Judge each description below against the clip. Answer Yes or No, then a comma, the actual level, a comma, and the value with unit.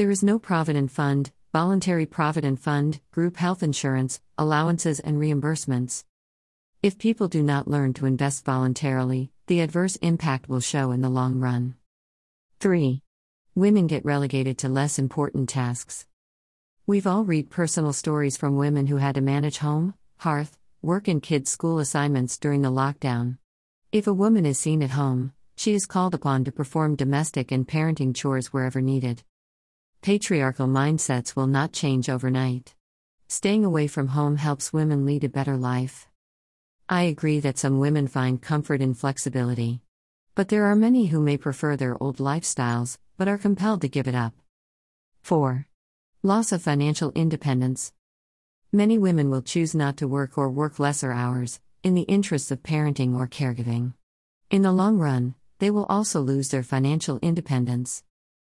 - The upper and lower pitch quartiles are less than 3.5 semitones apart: No, average, 3.8 semitones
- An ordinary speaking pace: Yes, average, 160 wpm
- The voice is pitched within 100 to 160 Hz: Yes, medium, 140 Hz